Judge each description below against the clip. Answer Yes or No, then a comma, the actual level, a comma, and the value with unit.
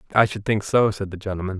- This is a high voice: No, low, 100 Hz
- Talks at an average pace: No, fast, 265 wpm